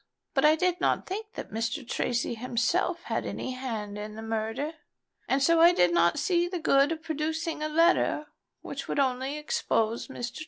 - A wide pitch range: Yes, wide, 6.1 semitones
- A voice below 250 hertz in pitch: No, very high, 275 Hz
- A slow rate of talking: No, average, 190 wpm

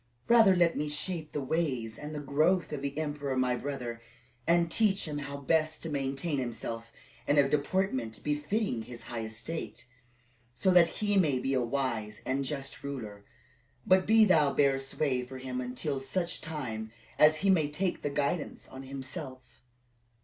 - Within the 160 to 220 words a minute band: Yes, average, 170 wpm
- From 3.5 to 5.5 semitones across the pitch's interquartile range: Yes, average, 4.0 semitones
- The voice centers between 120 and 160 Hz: Yes, medium, 140 Hz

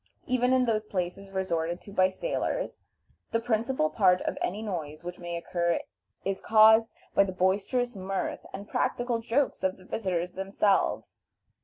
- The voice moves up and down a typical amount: Yes, average, 3.8 semitones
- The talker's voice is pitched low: No, high, 195 Hz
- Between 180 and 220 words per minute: No, average, 155 wpm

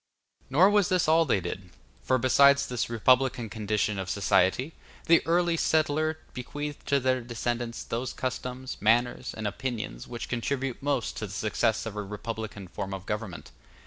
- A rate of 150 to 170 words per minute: Yes, average, 160 wpm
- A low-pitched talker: Yes, low, 120 Hz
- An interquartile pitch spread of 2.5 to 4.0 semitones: No, average, 4.6 semitones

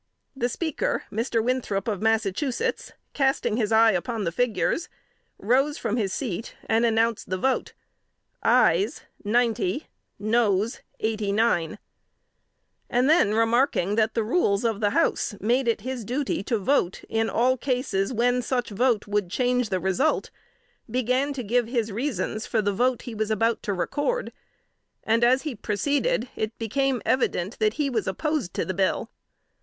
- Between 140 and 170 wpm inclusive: Yes, average, 155 wpm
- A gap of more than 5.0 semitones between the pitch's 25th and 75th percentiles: No, average, 3.4 semitones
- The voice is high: Yes, high, 230 Hz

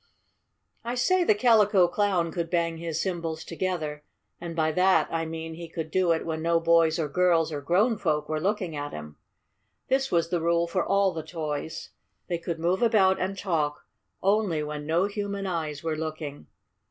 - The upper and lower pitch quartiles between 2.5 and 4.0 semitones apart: Yes, average, 3.0 semitones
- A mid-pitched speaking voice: Yes, medium, 170 Hz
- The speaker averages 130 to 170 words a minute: No, average, 185 wpm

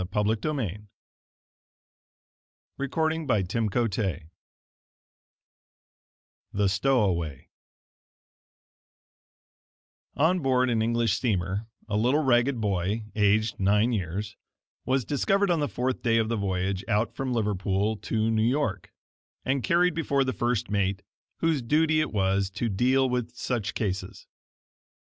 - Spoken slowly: Yes, slow, 120 wpm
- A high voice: No, low, 115 Hz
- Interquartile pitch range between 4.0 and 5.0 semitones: Yes, average, 4.6 semitones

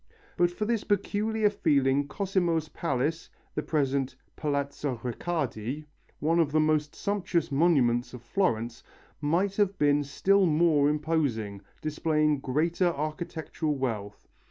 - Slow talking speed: Yes, slow, 120 wpm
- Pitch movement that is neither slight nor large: Yes, average, 4.0 semitones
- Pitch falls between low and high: Yes, medium, 155 Hz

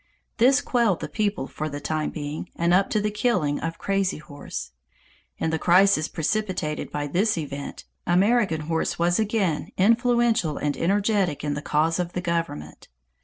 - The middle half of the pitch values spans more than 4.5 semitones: Yes, wide, 5.4 semitones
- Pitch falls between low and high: Yes, medium, 175 Hz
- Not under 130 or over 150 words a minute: No, average, 165 wpm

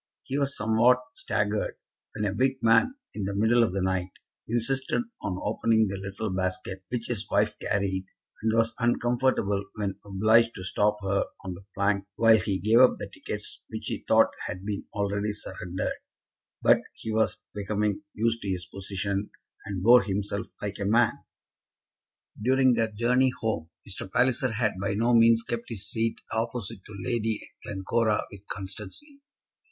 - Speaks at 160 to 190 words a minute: Yes, average, 165 wpm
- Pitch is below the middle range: Yes, low, 105 Hz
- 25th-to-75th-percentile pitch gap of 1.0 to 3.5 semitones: Yes, average, 2.8 semitones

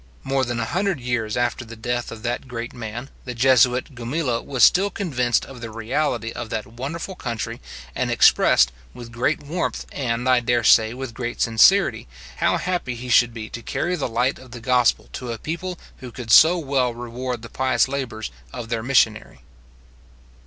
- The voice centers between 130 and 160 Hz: No, low, 120 Hz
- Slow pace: No, average, 185 wpm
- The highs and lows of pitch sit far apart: No, narrow, 2.5 semitones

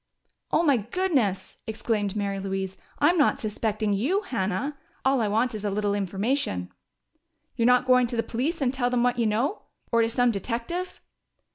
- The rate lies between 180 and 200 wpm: No, average, 170 wpm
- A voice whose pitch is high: Yes, high, 230 Hz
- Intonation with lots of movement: No, average, 4.3 semitones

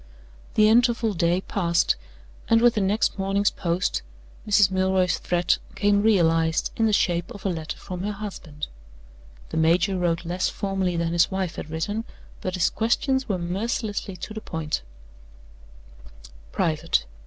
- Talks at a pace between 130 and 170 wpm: Yes, average, 150 wpm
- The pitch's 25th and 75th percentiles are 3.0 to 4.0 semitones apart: Yes, average, 3.6 semitones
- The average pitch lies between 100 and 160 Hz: No, high, 190 Hz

